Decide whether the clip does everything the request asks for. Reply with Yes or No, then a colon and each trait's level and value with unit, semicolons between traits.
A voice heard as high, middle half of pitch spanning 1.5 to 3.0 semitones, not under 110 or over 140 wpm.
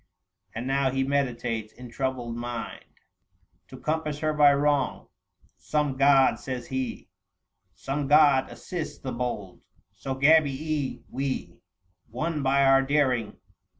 No: low, 135 Hz; average, 2.7 semitones; slow, 135 wpm